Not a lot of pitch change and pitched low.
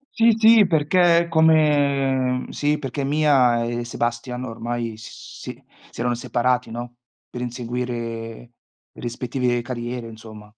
No: average, 3.5 semitones; low, 125 Hz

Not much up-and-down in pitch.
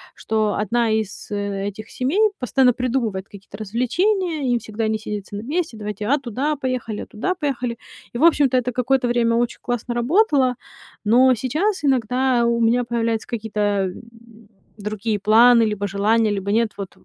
No: average, 3.4 semitones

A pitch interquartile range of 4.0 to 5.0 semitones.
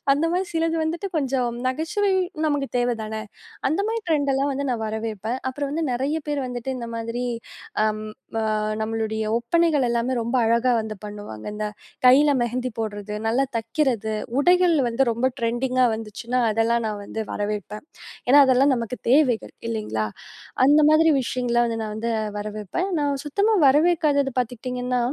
Yes: average, 4.3 semitones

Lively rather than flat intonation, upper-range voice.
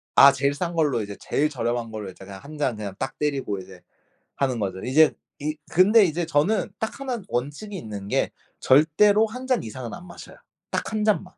No: wide, 7.9 semitones; medium, 145 Hz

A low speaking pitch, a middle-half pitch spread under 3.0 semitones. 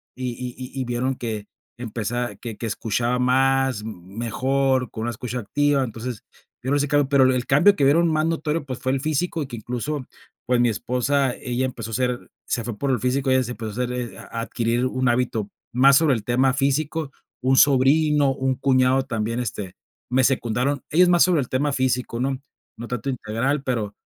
Yes: low, 130 Hz; narrow, 2.4 semitones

